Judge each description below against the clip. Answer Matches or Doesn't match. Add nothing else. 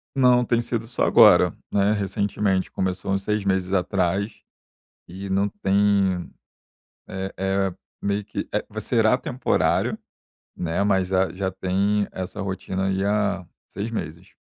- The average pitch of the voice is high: Doesn't match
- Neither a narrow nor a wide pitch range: Doesn't match